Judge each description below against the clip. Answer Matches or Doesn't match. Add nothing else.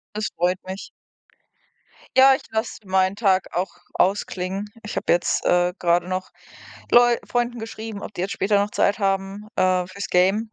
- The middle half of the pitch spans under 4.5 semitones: Matches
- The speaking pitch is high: Matches